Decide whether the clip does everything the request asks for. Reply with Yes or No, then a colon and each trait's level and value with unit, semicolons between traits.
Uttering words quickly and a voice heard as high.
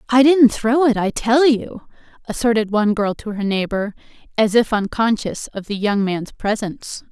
No: average, 175 wpm; high, 220 Hz